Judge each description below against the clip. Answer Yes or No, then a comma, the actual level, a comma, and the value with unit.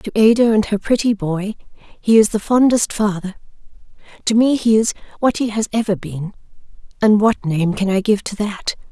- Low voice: No, high, 210 Hz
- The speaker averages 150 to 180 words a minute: No, average, 190 wpm